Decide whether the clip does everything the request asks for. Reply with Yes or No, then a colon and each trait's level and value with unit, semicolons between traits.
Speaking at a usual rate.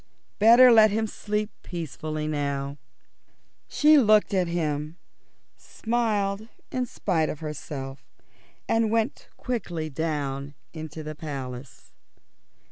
No: slow, 105 wpm